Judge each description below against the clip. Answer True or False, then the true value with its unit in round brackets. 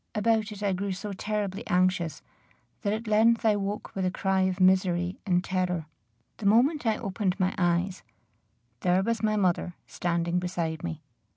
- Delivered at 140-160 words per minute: False (170 wpm)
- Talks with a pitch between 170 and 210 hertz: True (190 Hz)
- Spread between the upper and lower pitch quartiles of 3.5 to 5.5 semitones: False (2.8 semitones)